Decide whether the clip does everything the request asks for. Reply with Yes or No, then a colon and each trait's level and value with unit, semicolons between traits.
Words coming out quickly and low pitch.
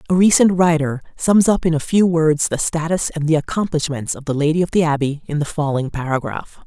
No: fast, 215 wpm; medium, 160 Hz